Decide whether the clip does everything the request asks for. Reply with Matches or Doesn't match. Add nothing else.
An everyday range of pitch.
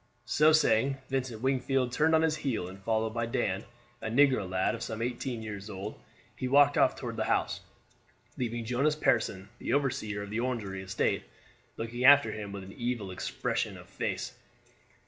Matches